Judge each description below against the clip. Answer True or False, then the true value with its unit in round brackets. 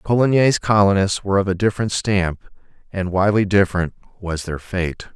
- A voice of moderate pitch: False (95 Hz)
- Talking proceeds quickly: False (150 wpm)